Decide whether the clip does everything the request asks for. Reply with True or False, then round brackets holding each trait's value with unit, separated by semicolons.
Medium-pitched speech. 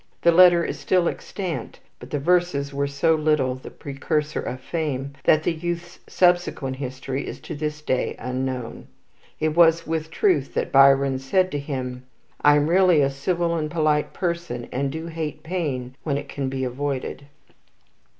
True (150 Hz)